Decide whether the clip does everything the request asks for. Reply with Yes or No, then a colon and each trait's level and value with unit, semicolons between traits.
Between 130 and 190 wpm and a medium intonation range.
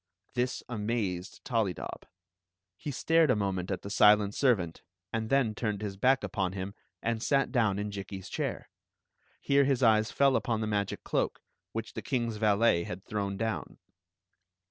Yes: average, 160 wpm; average, 3.5 semitones